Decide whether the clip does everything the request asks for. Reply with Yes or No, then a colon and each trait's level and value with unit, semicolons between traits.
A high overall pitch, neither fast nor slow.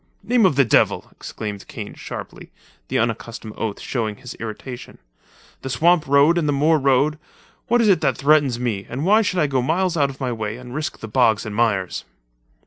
No: low, 135 Hz; average, 195 wpm